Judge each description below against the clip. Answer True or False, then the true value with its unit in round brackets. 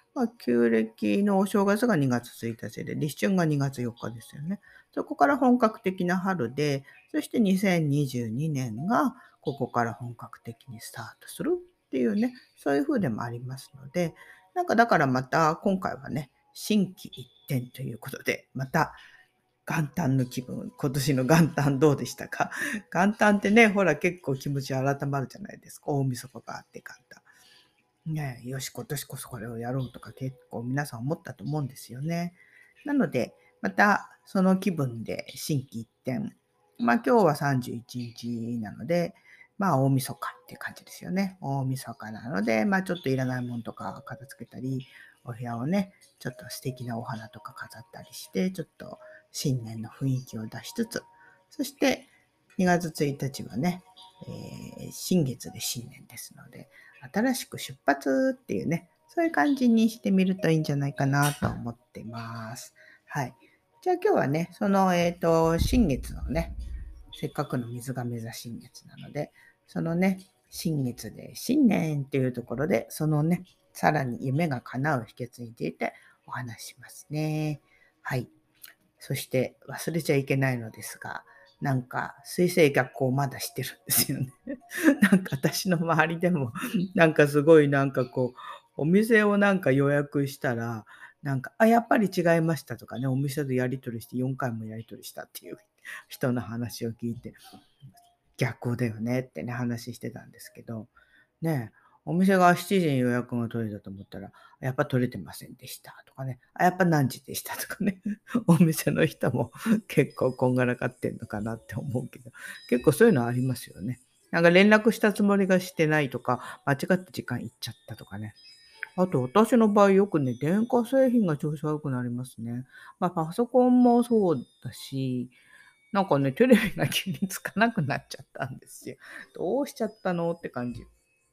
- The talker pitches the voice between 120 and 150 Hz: True (140 Hz)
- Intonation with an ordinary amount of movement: False (7.3 semitones)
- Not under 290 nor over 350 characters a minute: True (320 characters per minute)